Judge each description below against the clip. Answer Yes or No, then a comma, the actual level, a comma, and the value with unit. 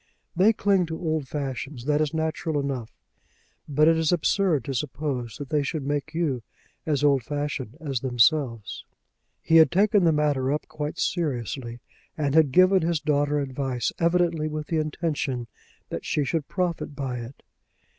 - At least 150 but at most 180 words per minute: Yes, average, 165 wpm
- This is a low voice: No, medium, 150 Hz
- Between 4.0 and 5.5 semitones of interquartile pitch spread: No, average, 3.1 semitones